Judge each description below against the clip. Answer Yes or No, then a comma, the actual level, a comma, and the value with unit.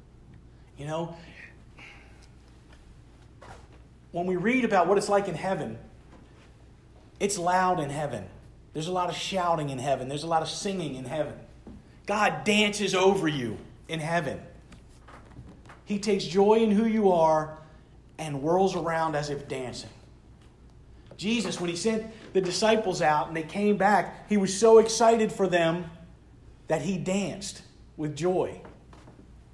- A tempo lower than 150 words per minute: Yes, average, 140 wpm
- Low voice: No, medium, 175 Hz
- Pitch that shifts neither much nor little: Yes, average, 4.8 semitones